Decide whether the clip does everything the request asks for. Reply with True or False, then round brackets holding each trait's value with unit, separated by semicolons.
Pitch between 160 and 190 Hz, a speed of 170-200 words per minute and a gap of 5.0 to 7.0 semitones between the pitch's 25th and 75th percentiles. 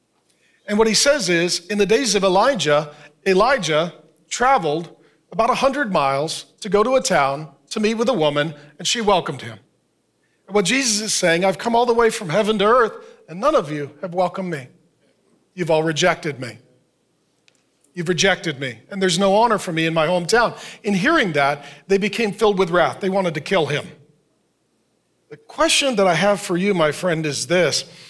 True (185 Hz; 190 wpm; 5.3 semitones)